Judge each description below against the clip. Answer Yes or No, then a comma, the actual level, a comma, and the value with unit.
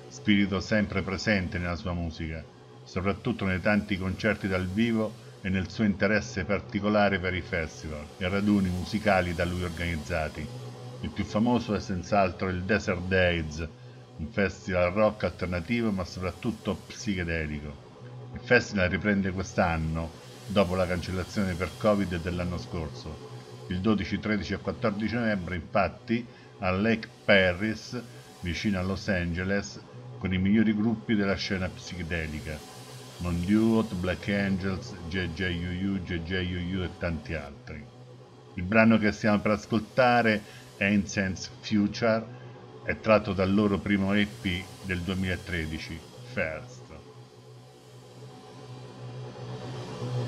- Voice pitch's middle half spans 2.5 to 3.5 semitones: No, average, 4.4 semitones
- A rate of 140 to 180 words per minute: No, average, 120 wpm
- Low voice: Yes, very low, 95 Hz